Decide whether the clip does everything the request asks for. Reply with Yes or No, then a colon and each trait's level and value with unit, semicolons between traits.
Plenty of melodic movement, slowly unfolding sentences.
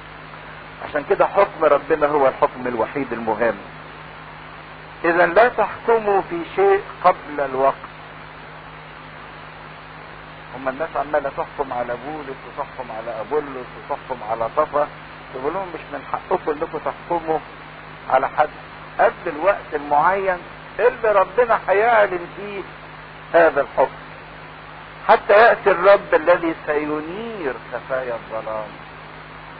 Yes: wide, 8.6 semitones; slow, 105 wpm